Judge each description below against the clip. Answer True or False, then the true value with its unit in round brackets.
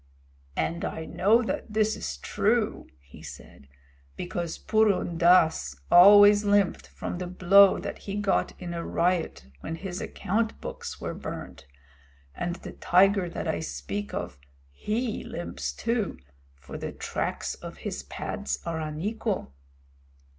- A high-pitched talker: False (180 Hz)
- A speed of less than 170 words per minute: True (140 wpm)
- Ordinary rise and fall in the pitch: True (4.4 semitones)